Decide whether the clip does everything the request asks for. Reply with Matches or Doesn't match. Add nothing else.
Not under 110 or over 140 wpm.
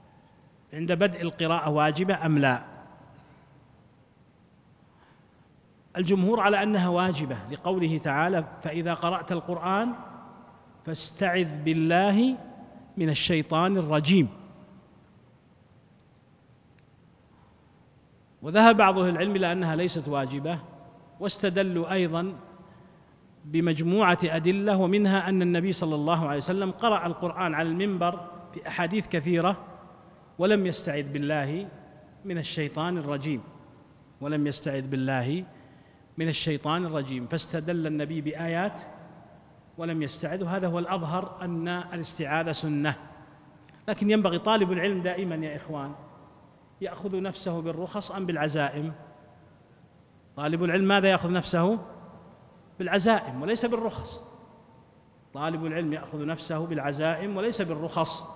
Doesn't match